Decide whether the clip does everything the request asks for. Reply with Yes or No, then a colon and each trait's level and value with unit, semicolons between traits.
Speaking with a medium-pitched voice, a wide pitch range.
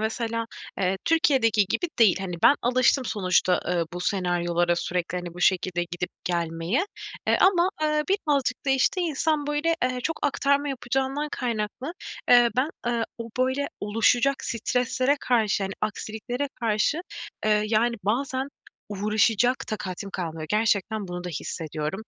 No: high, 225 Hz; wide, 6.2 semitones